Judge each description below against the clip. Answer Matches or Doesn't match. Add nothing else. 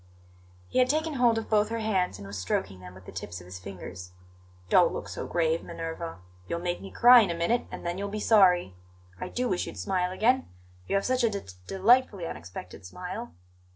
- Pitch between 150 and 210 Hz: Matches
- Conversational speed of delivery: Doesn't match